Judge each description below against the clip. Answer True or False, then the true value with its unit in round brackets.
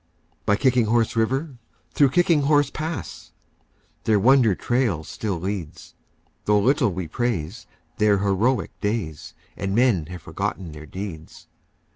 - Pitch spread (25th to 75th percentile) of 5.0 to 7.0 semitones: True (5.5 semitones)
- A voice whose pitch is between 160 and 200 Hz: False (105 Hz)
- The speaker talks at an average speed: False (130 wpm)